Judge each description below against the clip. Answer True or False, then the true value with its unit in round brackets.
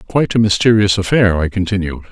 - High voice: False (100 Hz)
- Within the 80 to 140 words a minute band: False (170 wpm)